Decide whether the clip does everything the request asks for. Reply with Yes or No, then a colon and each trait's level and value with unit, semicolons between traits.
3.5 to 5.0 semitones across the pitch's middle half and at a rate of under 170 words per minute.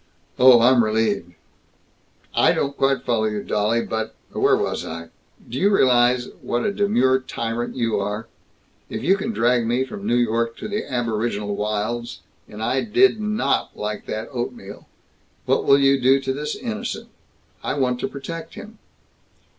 Yes: average, 3.8 semitones; average, 160 wpm